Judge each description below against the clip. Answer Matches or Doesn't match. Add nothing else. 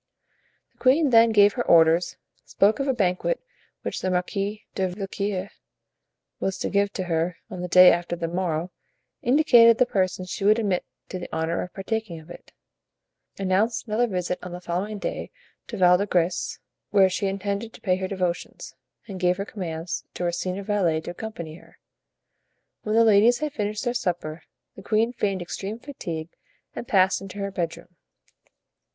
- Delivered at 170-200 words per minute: Matches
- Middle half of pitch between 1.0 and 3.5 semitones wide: Matches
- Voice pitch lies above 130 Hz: Matches